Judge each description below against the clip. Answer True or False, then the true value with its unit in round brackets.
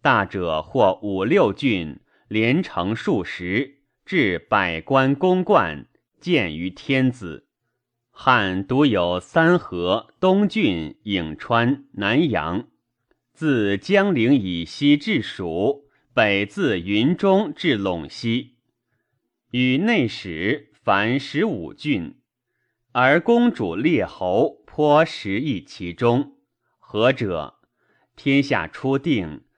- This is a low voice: True (125 Hz)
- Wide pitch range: True (6.1 semitones)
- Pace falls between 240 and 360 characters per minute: False (135 characters per minute)